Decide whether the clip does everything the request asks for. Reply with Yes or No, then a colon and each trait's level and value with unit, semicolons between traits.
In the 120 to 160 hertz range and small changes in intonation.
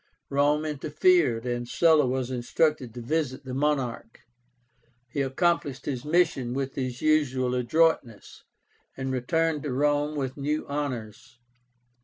No: medium, 140 Hz; average, 3.2 semitones